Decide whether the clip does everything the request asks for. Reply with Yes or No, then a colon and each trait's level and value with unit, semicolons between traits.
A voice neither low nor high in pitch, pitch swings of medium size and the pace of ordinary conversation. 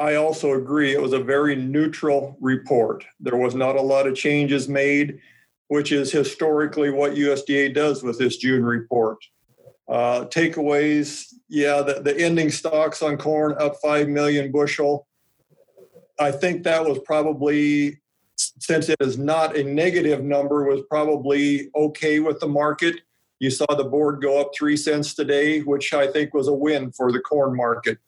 No: medium, 145 Hz; narrow, 1.4 semitones; average, 165 wpm